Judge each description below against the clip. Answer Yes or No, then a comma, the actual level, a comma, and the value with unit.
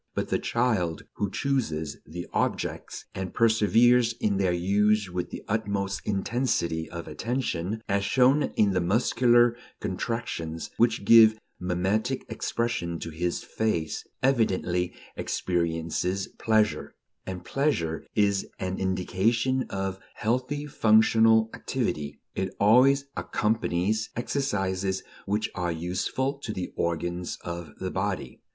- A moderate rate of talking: No, slow, 120 wpm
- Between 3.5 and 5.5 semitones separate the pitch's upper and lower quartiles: Yes, average, 4.6 semitones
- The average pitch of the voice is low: Yes, low, 100 Hz